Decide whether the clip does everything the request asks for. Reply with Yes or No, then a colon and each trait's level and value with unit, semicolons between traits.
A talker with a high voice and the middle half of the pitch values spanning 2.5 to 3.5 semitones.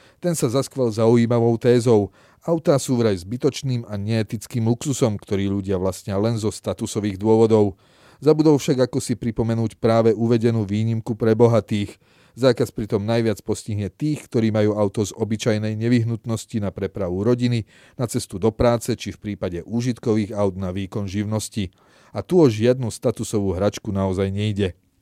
No: low, 110 Hz; average, 2.8 semitones